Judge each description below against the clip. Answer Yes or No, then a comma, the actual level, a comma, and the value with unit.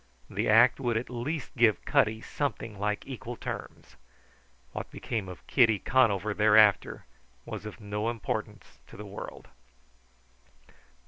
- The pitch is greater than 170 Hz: No, low, 110 Hz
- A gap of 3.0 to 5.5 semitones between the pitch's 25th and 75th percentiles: No, narrow, 2.5 semitones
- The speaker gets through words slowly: Yes, slow, 130 wpm